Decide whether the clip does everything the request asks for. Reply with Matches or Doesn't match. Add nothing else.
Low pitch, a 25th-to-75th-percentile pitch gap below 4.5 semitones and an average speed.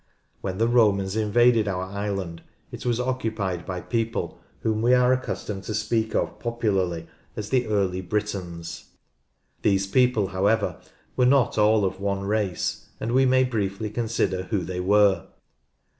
Matches